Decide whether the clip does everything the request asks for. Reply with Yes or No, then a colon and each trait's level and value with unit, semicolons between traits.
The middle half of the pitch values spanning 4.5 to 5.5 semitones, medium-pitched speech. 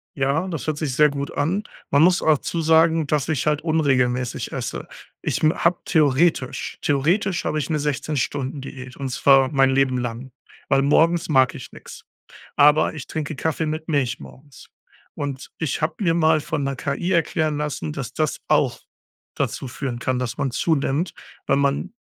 No: average, 2.9 semitones; medium, 145 Hz